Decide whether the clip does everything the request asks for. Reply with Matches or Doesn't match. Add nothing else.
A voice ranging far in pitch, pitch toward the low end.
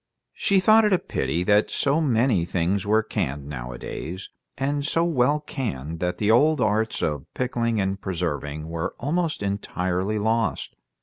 Matches